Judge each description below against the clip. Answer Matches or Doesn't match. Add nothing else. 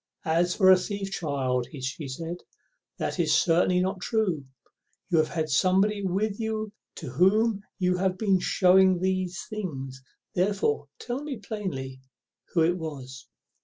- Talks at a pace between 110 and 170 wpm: Matches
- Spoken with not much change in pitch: Doesn't match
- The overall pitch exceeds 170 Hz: Matches